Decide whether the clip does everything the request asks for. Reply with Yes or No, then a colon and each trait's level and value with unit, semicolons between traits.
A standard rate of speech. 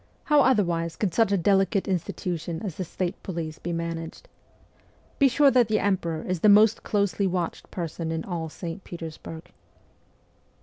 Yes: average, 160 wpm